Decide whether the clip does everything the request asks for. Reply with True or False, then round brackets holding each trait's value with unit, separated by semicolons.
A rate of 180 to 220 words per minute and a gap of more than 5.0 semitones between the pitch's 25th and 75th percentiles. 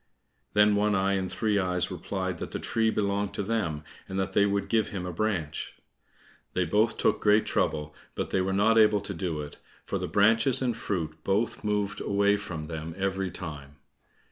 False (195 wpm; 2.5 semitones)